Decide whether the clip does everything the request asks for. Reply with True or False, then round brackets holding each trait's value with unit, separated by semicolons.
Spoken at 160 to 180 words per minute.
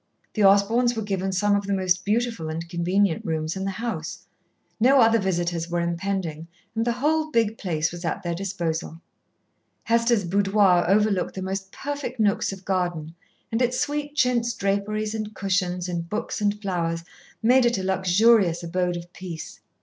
True (170 wpm)